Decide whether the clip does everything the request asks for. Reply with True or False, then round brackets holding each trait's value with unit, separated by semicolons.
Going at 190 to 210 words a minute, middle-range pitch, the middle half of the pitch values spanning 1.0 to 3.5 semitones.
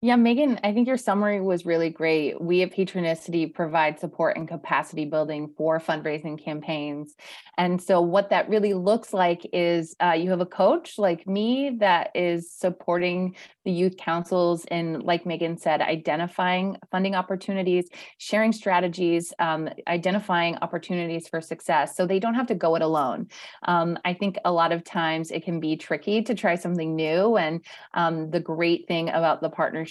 False (175 wpm; 175 Hz; 2.5 semitones)